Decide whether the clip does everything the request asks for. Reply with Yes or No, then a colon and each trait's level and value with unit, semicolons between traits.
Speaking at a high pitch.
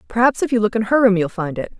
Yes: high, 220 Hz